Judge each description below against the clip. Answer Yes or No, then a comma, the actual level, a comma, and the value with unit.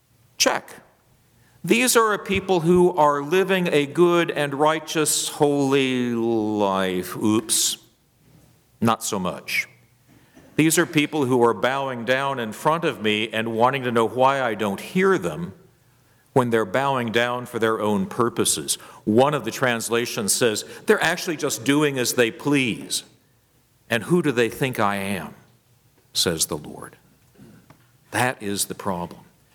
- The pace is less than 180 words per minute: Yes, average, 145 wpm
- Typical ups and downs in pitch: Yes, average, 4.6 semitones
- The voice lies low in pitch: Yes, low, 130 Hz